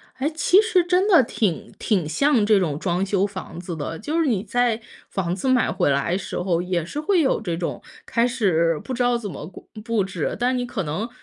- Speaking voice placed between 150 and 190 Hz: No, high, 205 Hz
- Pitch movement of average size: No, wide, 6.4 semitones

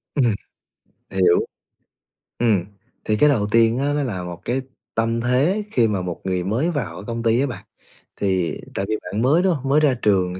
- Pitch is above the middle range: No, low, 115 Hz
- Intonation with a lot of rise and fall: Yes, wide, 5.9 semitones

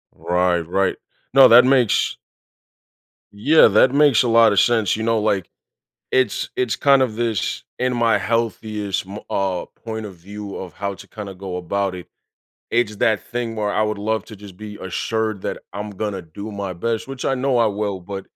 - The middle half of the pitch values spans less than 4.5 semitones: Yes, average, 2.9 semitones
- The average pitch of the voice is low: Yes, low, 105 Hz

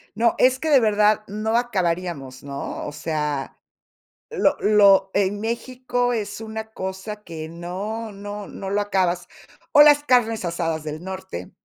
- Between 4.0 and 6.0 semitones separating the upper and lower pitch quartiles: Yes, average, 4.5 semitones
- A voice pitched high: Yes, high, 205 Hz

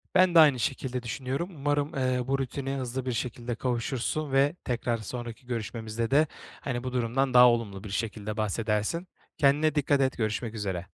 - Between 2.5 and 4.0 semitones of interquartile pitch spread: Yes, average, 3.1 semitones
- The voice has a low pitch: Yes, low, 125 Hz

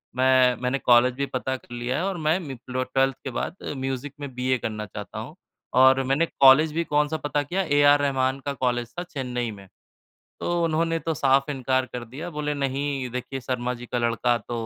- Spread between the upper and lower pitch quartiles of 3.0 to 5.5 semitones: No, narrow, 2.6 semitones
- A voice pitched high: No, low, 130 Hz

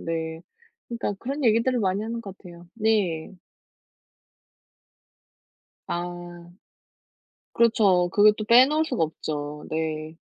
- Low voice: No, high, 190 Hz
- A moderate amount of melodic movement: No, wide, 5.9 semitones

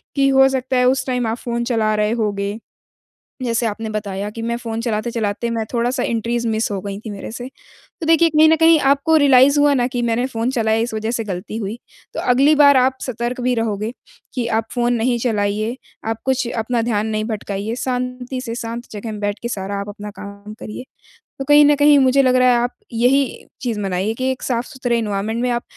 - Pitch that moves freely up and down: No, average, 2.9 semitones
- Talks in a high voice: Yes, high, 235 Hz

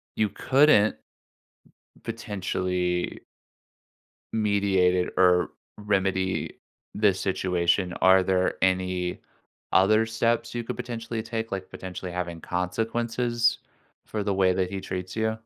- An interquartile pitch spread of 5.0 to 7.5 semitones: No, average, 3.3 semitones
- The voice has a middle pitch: No, very low, 95 Hz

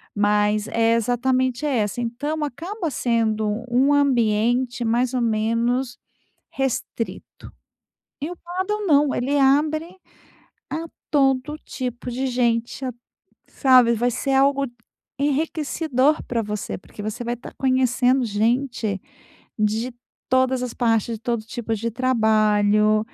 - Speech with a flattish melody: No, average, 3.2 semitones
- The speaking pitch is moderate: No, high, 245 Hz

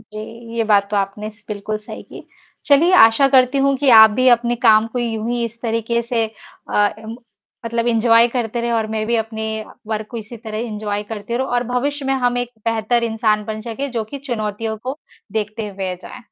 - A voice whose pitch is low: No, high, 230 Hz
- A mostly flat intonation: Yes, narrow, 2.0 semitones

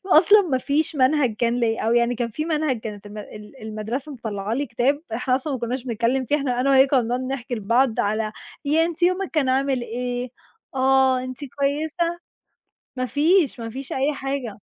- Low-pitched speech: No, very high, 260 Hz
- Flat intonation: No, average, 3.4 semitones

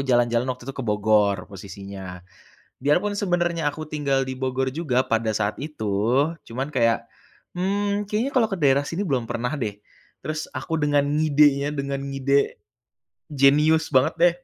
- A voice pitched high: No, medium, 140 Hz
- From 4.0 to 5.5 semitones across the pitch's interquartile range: Yes, average, 4.6 semitones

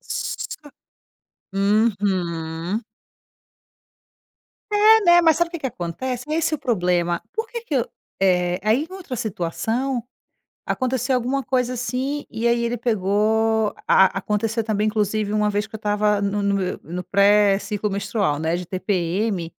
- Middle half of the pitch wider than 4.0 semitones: Yes, average, 4.5 semitones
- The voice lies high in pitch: Yes, high, 215 Hz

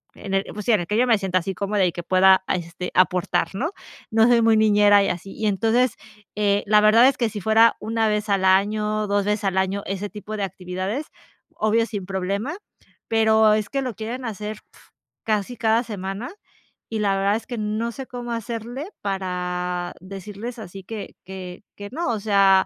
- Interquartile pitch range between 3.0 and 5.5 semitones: No, narrow, 2.6 semitones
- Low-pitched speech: No, high, 210 Hz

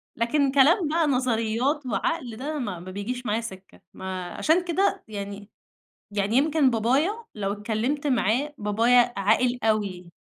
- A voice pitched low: No, high, 235 Hz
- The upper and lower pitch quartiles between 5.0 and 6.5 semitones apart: Yes, wide, 5.4 semitones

